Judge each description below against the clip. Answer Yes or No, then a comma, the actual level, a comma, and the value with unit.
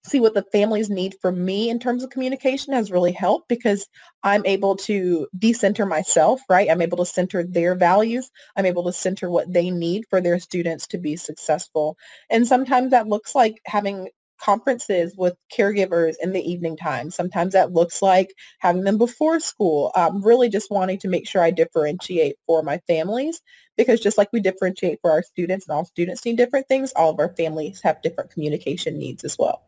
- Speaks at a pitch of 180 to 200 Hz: Yes, high, 190 Hz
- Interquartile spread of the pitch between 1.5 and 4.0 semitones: No, average, 4.6 semitones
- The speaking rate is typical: Yes, average, 195 wpm